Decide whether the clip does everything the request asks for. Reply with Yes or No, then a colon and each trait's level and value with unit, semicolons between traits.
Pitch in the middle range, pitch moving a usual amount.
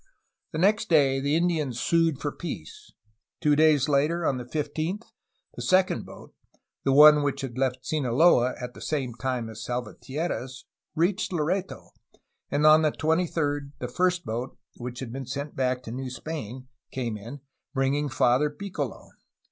Yes: medium, 145 Hz; average, 3.8 semitones